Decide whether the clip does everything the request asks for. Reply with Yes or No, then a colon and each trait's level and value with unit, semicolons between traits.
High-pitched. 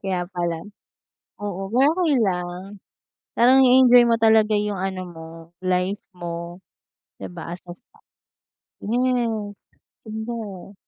Yes: high, 205 Hz